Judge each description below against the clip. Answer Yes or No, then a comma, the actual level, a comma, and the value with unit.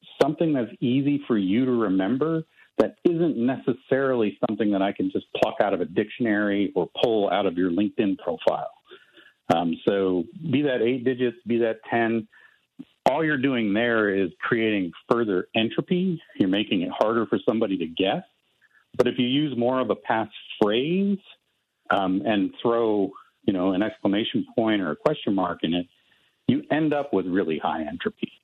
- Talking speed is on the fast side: No, average, 175 wpm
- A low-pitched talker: Yes, low, 120 Hz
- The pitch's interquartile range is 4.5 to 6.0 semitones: Yes, average, 5.2 semitones